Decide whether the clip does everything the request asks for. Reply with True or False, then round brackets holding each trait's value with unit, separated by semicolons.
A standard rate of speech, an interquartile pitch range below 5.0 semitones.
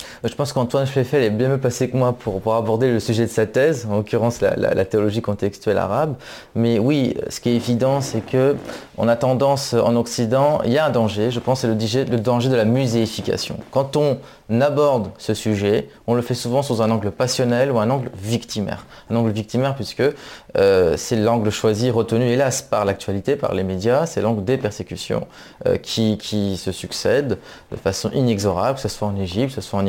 True (210 wpm; 3.2 semitones)